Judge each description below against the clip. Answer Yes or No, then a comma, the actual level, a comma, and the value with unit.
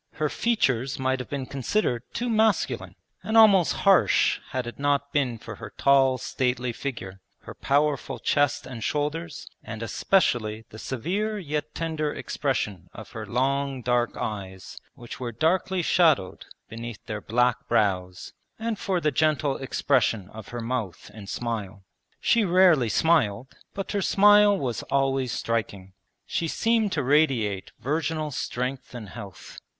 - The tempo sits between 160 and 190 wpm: No, average, 145 wpm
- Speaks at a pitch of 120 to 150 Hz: Yes, low, 135 Hz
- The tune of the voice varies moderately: No, wide, 5.8 semitones